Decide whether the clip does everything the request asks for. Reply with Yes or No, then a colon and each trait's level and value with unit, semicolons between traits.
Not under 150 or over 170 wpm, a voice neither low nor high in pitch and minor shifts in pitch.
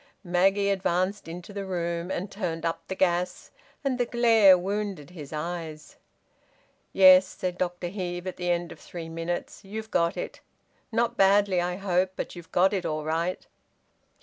Yes: average, 165 wpm; medium, 180 Hz; narrow, 2.3 semitones